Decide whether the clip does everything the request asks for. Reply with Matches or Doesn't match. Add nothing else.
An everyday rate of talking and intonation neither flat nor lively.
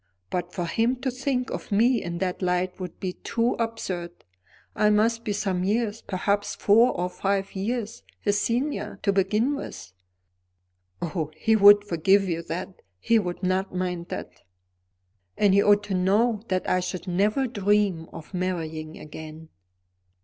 Matches